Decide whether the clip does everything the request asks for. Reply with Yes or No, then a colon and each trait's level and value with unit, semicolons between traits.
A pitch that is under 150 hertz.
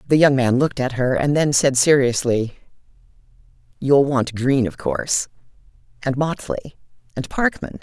Yes: low, 135 Hz